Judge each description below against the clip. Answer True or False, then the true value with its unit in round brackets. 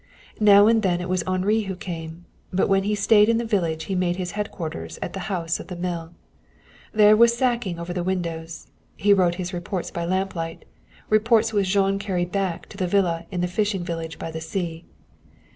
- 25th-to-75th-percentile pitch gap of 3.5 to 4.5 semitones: False (3.0 semitones)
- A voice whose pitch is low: False (185 Hz)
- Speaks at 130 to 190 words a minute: False (200 wpm)